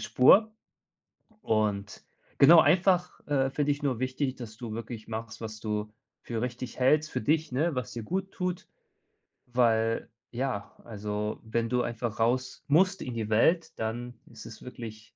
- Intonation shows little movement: No, average, 4.6 semitones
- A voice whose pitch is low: Yes, low, 120 Hz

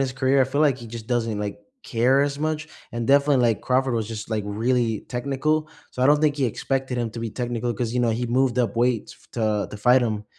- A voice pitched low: Yes, low, 120 Hz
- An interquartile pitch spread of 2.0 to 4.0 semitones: Yes, average, 2.8 semitones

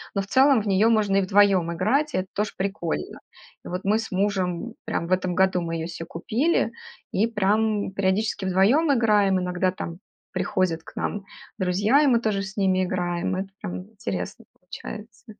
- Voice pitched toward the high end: Yes, high, 195 Hz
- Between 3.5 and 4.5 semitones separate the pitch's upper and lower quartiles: No, average, 2.8 semitones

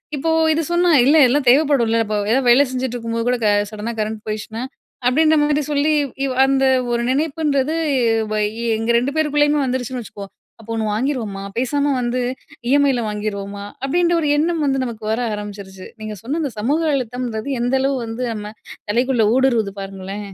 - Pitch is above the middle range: Yes, very high, 250 Hz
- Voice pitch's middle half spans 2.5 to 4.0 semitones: No, average, 4.7 semitones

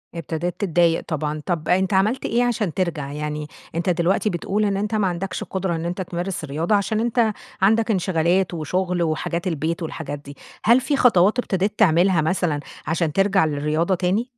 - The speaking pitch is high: No, medium, 180 Hz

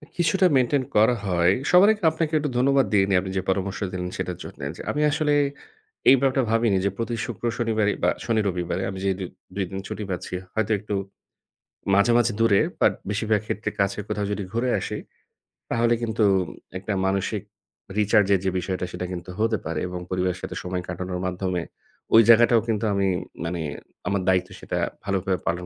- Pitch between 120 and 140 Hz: No, low, 100 Hz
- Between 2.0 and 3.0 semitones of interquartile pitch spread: No, average, 4.0 semitones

